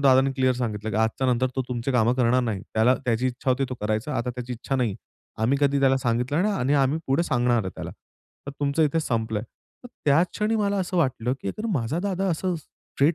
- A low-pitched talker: Yes, low, 130 Hz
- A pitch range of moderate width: Yes, average, 3.6 semitones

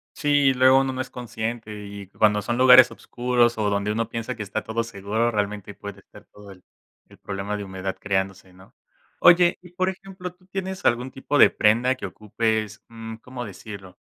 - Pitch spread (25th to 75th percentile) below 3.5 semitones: No, average, 4.0 semitones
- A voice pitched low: Yes, low, 115 Hz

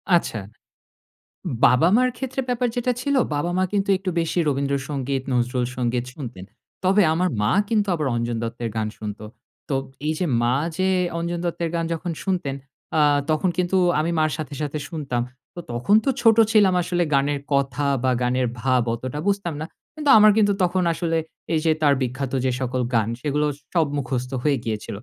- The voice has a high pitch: No, medium, 150 Hz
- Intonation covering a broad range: Yes, wide, 6.3 semitones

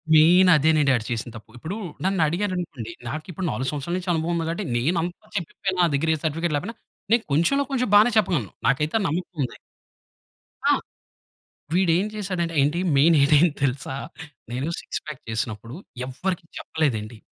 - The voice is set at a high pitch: No, medium, 160 Hz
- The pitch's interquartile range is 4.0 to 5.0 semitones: Yes, average, 4.6 semitones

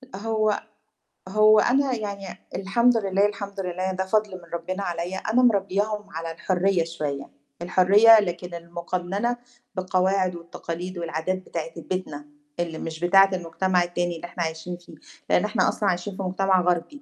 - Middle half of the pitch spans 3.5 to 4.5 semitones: No, narrow, 2.6 semitones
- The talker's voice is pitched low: No, medium, 185 Hz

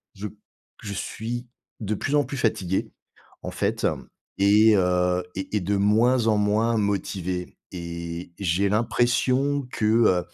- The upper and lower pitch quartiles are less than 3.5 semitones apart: No, average, 3.9 semitones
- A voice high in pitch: No, low, 105 Hz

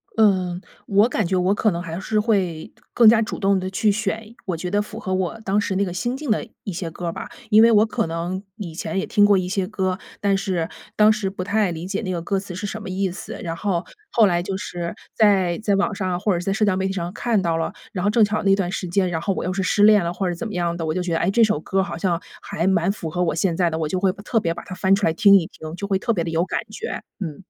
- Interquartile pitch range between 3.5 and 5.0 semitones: No, average, 2.8 semitones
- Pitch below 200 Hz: Yes, high, 190 Hz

